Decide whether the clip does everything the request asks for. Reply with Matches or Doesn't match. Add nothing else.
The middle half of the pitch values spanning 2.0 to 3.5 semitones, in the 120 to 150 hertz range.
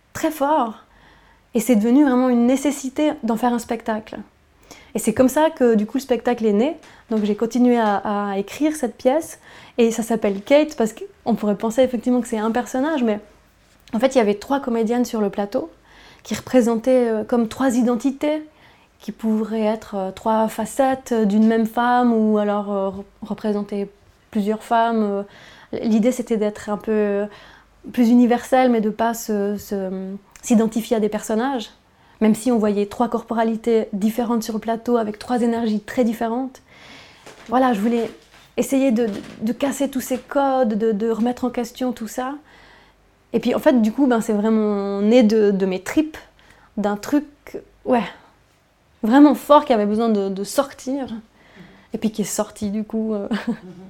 Doesn't match